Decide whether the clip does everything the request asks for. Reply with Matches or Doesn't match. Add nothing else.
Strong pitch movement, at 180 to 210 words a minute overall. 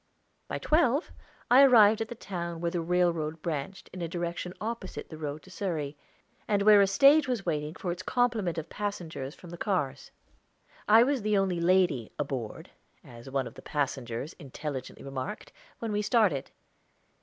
Doesn't match